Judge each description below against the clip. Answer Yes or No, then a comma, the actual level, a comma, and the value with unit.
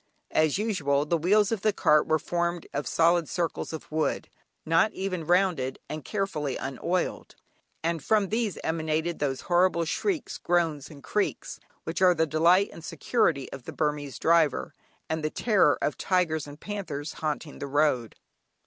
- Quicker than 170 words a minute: No, average, 160 wpm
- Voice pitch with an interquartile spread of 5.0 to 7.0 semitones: No, average, 3.6 semitones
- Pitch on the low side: No, medium, 160 Hz